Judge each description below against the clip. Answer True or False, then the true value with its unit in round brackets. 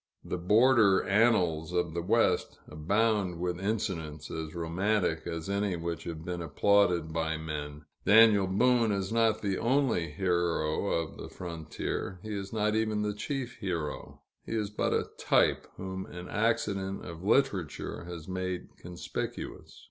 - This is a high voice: False (95 Hz)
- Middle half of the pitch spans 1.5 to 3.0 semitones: False (4.0 semitones)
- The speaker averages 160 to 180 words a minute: False (150 wpm)